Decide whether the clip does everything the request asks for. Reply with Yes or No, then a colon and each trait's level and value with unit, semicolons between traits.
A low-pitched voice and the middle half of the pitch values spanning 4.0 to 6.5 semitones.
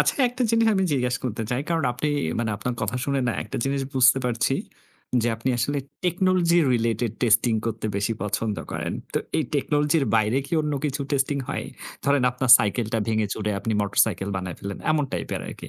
Yes: low, 125 Hz; average, 4.5 semitones